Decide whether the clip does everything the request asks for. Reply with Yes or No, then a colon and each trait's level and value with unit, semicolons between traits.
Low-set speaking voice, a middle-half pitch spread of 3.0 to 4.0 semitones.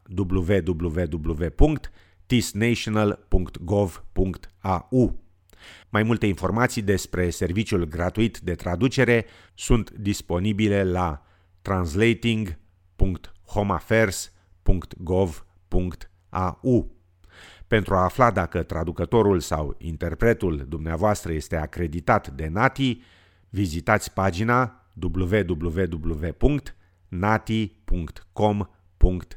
Yes: very low, 95 Hz; average, 3.5 semitones